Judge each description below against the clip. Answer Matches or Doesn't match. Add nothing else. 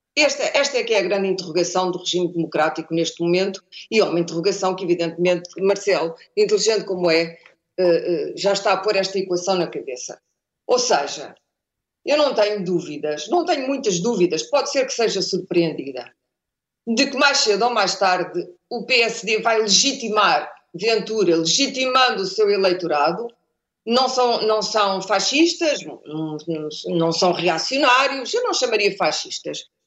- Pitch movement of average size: Doesn't match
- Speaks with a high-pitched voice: Matches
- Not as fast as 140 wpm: Doesn't match